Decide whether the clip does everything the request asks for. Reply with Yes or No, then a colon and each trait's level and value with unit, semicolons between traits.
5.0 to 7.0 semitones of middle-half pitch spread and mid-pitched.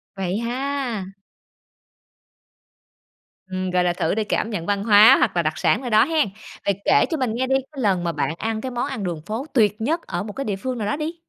No: wide, 5.4 semitones; high, 215 Hz